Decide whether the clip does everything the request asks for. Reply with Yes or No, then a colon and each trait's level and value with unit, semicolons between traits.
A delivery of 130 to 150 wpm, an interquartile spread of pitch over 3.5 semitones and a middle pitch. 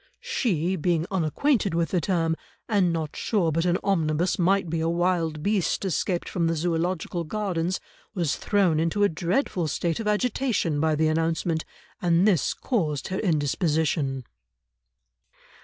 No: average, 145 wpm; average, 3.2 semitones; medium, 170 Hz